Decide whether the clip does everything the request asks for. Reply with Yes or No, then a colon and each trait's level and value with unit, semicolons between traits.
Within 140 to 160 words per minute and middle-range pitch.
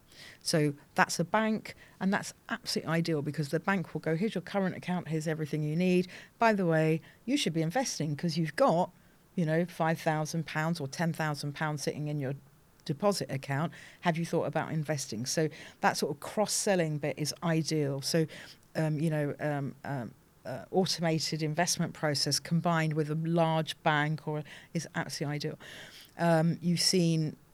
No: average, 175 wpm; medium, 160 Hz